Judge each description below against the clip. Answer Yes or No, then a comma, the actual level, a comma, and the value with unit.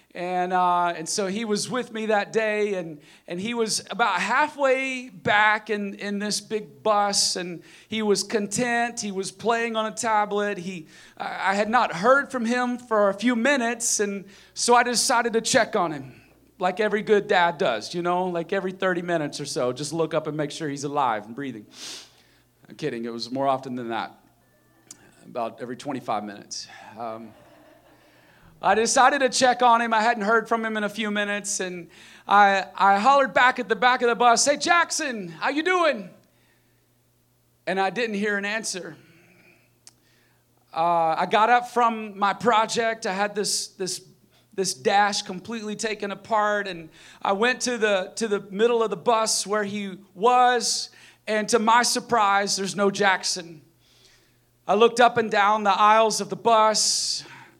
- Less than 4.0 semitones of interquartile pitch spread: No, average, 4.3 semitones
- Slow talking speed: No, average, 180 wpm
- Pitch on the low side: No, high, 205 Hz